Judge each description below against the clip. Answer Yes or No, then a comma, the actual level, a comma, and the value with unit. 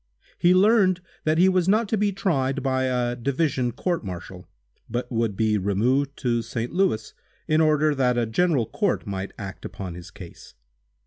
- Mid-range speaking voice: No, low, 130 Hz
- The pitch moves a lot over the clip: Yes, wide, 7.4 semitones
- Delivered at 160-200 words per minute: Yes, average, 175 wpm